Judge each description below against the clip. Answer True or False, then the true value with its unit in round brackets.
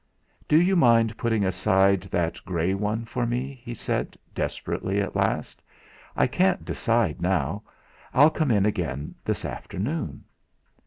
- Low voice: True (105 Hz)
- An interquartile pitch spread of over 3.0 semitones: True (4.7 semitones)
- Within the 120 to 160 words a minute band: True (140 wpm)